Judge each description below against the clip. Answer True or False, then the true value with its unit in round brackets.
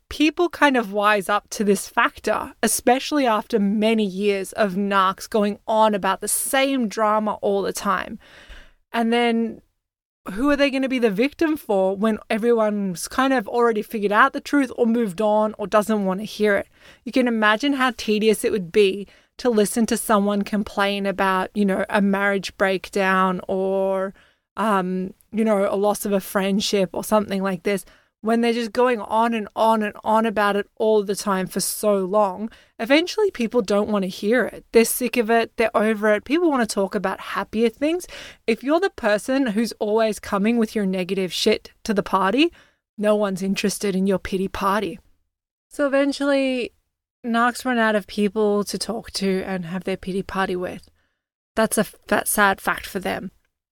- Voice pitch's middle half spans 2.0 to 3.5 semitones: True (2.8 semitones)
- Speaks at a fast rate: False (185 wpm)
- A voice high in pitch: True (215 Hz)